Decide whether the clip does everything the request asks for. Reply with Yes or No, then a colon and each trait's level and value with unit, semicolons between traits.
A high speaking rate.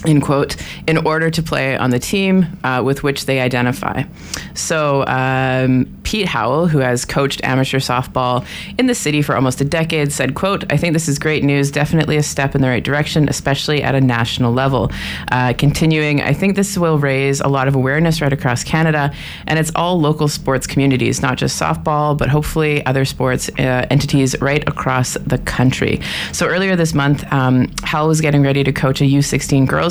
No: average, 195 wpm